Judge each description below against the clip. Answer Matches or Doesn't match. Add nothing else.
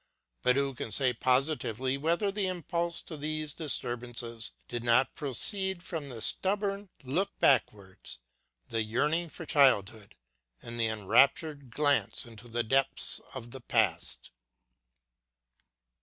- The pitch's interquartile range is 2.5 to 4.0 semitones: Doesn't match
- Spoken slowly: Matches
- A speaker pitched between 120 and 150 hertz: Matches